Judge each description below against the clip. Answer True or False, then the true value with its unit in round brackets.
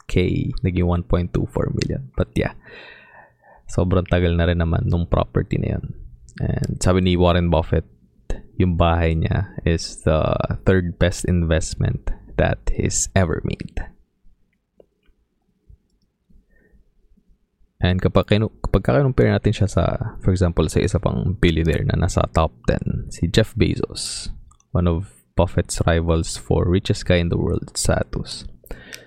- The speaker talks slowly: True (130 wpm)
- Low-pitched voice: True (90 Hz)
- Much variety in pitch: False (3.2 semitones)